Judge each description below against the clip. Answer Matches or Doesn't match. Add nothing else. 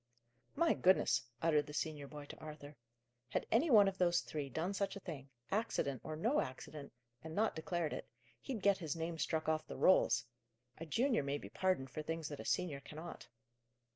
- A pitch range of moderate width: Matches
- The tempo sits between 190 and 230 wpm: Matches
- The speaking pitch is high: Doesn't match